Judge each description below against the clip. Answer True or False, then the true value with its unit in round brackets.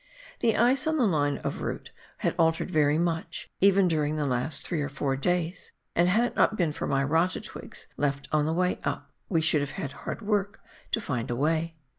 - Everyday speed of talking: False (215 wpm)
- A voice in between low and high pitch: True (160 Hz)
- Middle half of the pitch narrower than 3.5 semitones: False (4.2 semitones)